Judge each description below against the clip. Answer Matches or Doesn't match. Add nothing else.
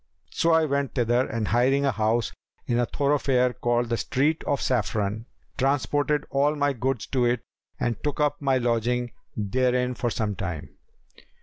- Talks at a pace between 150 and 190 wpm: Matches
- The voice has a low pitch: Matches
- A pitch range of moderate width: Matches